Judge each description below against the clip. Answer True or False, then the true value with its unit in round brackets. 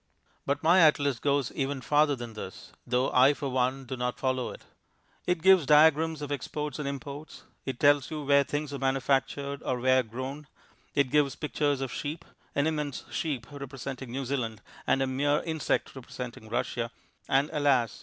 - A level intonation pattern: True (2.3 semitones)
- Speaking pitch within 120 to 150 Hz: True (140 Hz)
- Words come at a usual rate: True (175 wpm)